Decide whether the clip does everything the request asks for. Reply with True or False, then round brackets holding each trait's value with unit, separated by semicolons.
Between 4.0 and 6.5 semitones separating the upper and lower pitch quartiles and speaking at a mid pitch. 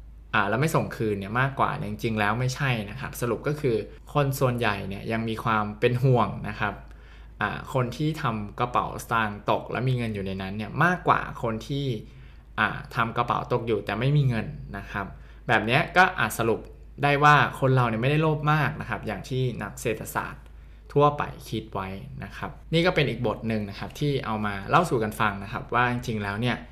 False (4.6 semitones; 115 Hz)